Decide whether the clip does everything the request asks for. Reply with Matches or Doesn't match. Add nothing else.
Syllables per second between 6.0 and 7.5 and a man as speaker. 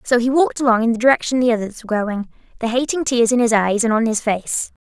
Doesn't match